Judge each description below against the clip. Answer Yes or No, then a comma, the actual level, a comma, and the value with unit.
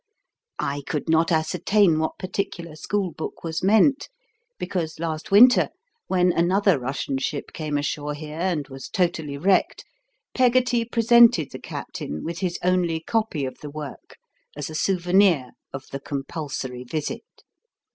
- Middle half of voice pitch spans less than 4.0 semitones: No, average, 4.7 semitones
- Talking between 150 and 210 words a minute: No, average, 140 wpm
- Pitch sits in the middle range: Yes, medium, 165 Hz